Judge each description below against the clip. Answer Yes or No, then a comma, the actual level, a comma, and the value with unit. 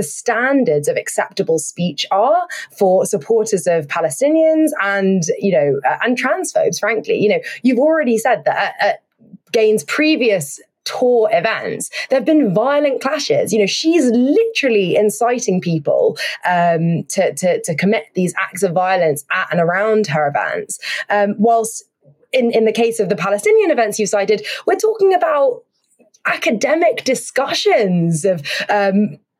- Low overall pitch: No, high, 225 Hz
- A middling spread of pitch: No, wide, 7.6 semitones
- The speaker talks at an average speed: Yes, average, 145 wpm